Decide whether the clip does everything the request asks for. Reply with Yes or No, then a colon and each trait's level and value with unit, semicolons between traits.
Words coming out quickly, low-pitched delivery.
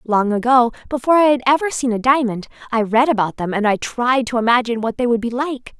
No: fast, 240 wpm; high, 245 Hz